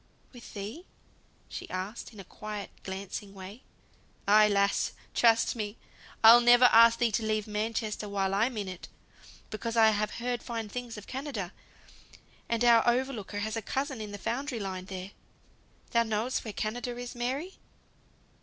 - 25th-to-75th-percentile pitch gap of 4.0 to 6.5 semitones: No, average, 2.8 semitones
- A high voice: Yes, high, 220 Hz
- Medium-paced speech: Yes, average, 155 wpm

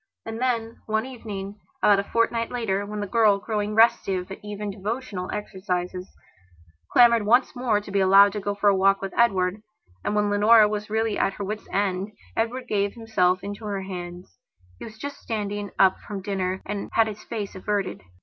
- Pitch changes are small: Yes, narrow, 2.3 semitones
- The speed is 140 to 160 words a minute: No, average, 190 wpm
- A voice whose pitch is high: Yes, high, 205 Hz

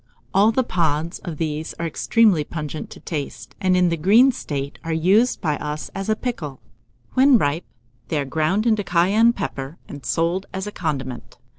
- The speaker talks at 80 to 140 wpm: No, average, 185 wpm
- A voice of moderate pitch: Yes, medium, 170 Hz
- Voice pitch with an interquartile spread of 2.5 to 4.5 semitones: No, wide, 5.4 semitones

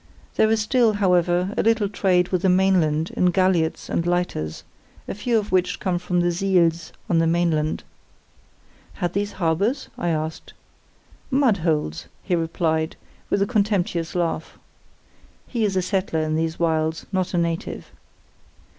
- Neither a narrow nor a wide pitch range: Yes, average, 3.2 semitones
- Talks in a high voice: No, medium, 180 Hz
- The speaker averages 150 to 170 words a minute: Yes, average, 155 wpm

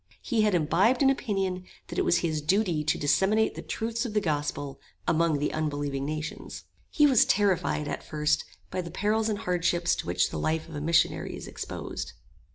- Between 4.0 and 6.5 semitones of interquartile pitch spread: Yes, wide, 5.6 semitones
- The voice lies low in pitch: No, medium, 170 Hz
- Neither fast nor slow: Yes, average, 190 wpm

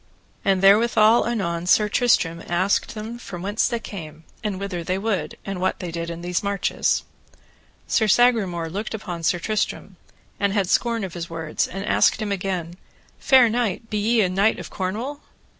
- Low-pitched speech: No, high, 195 Hz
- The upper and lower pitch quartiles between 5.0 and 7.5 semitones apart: No, average, 3.8 semitones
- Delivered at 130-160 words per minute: No, average, 175 wpm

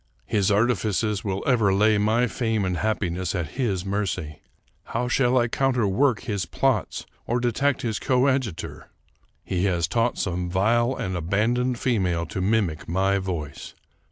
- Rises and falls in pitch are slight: No, average, 4.5 semitones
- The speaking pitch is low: Yes, low, 105 Hz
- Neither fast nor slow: Yes, average, 155 wpm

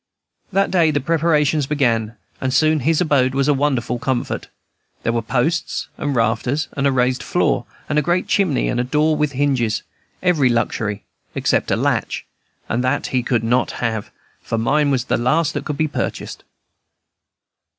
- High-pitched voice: No, low, 135 Hz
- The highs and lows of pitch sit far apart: No, average, 3.8 semitones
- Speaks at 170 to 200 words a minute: Yes, average, 175 wpm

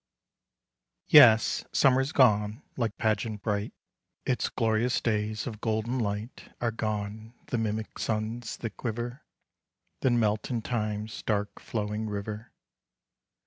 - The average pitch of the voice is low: Yes, low, 110 Hz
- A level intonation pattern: Yes, narrow, 2.0 semitones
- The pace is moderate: No, slow, 115 wpm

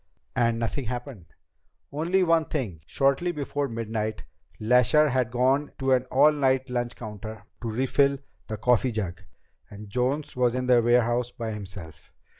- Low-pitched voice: Yes, low, 125 Hz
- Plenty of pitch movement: No, average, 3.6 semitones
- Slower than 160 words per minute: Yes, average, 150 wpm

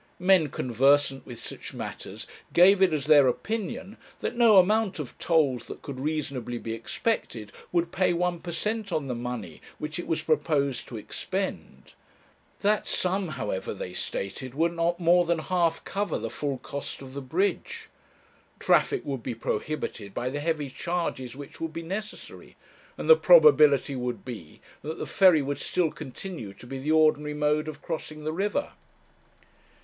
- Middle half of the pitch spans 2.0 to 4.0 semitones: No, average, 5.2 semitones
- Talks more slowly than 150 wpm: No, average, 165 wpm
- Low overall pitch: No, medium, 155 Hz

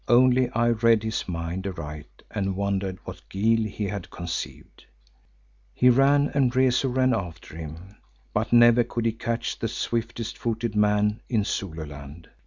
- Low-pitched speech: Yes, low, 110 Hz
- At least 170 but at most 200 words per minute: No, average, 150 wpm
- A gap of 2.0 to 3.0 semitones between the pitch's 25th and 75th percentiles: No, average, 4.0 semitones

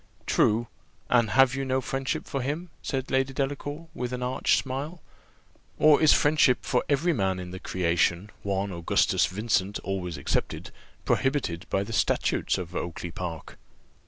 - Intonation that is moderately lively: No, wide, 6.4 semitones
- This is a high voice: No, low, 125 Hz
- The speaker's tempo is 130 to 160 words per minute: Yes, average, 155 wpm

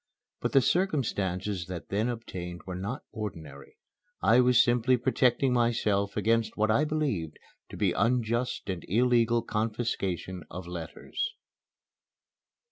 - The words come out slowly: Yes, slow, 125 wpm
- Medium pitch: No, low, 110 Hz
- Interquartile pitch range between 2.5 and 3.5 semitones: No, average, 4.9 semitones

